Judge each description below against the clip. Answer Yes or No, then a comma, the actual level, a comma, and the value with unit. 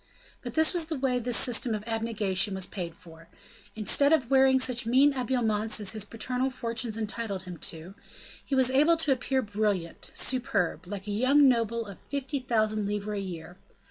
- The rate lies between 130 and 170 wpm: No, average, 180 wpm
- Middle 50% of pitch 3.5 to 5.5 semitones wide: Yes, average, 4.3 semitones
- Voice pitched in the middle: No, high, 225 Hz